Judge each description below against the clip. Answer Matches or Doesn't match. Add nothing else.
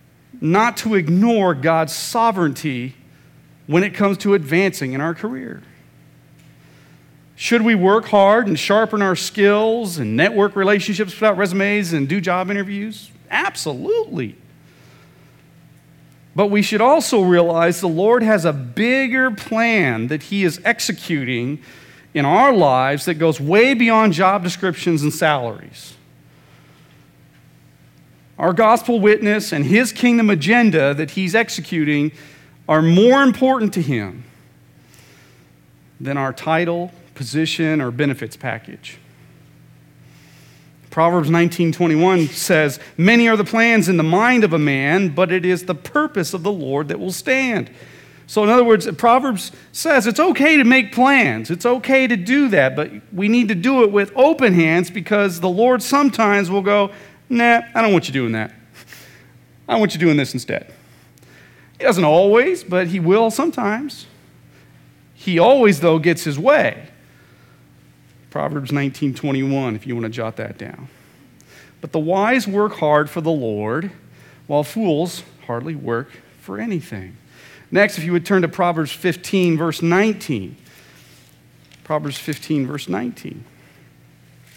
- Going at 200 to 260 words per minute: Doesn't match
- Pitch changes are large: Matches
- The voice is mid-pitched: Matches